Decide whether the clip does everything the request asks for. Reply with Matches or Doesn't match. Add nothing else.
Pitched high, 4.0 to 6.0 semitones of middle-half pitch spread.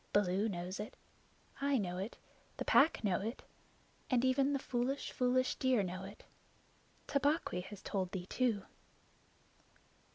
Matches